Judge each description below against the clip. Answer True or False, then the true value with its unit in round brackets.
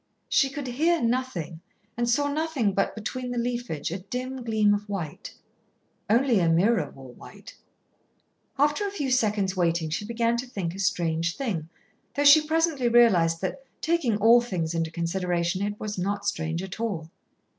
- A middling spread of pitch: False (6.5 semitones)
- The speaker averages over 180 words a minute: False (165 wpm)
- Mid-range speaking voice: False (210 Hz)